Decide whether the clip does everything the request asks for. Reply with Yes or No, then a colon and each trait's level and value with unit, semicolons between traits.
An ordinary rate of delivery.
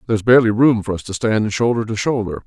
No: fast, 270 wpm